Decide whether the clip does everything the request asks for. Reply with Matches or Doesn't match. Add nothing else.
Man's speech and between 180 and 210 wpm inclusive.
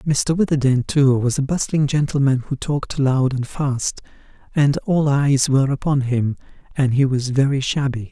Doesn't match